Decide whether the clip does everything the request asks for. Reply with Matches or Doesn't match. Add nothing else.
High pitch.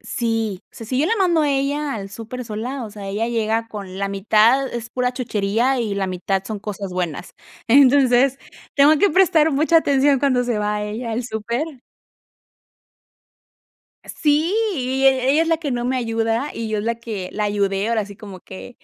Matches